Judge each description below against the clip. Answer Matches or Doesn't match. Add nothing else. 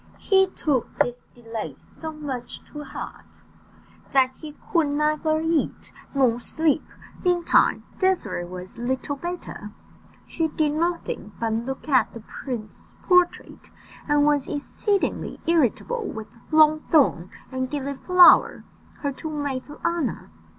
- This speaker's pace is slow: Matches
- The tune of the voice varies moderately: Matches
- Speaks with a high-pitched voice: Matches